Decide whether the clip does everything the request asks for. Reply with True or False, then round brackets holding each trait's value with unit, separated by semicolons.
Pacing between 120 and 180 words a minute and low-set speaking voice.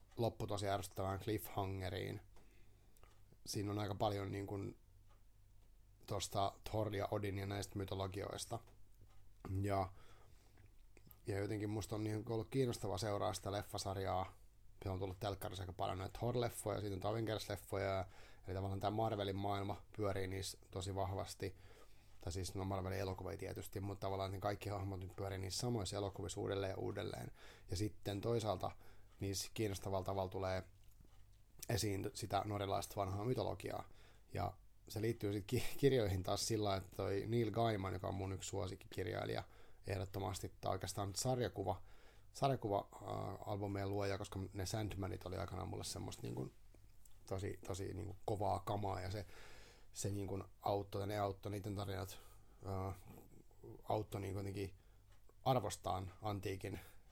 True (135 wpm; 100 Hz)